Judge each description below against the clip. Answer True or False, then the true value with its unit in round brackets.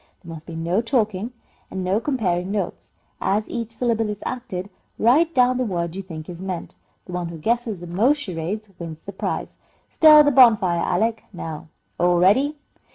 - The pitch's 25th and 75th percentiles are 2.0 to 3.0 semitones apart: False (5.1 semitones)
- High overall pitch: True (200 Hz)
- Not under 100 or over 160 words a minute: False (180 wpm)